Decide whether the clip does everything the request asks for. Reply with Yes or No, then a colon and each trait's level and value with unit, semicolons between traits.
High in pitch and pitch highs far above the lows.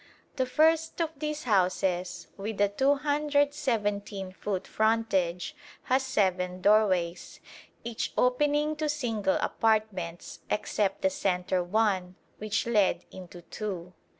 Yes: high, 210 Hz; wide, 6.5 semitones